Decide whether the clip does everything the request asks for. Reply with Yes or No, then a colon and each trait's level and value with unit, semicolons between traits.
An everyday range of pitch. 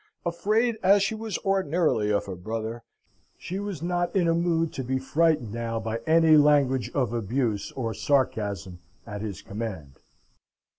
No: wide, 7.6 semitones